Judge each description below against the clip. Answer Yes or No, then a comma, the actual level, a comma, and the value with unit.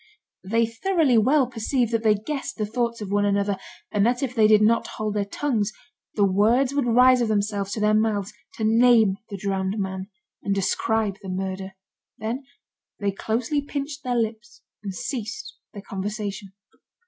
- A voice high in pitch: Yes, high, 215 Hz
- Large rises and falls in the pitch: No, average, 3.2 semitones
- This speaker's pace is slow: No, average, 170 wpm